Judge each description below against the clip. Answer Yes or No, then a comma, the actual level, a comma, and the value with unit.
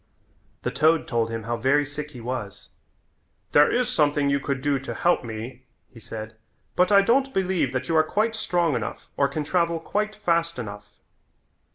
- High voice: No, medium, 145 Hz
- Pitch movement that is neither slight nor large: No, wide, 6.0 semitones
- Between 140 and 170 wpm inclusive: No, average, 185 wpm